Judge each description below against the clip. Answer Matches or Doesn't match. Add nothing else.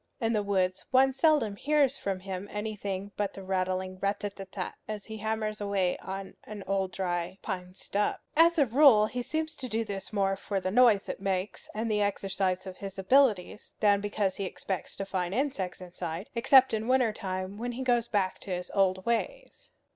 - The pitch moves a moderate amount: Matches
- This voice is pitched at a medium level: Doesn't match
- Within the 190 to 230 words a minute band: Matches